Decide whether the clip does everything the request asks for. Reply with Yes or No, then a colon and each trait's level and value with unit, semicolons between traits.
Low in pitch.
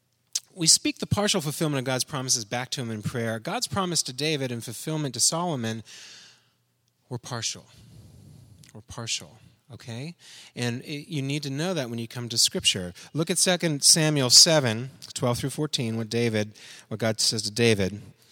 Yes: low, 130 Hz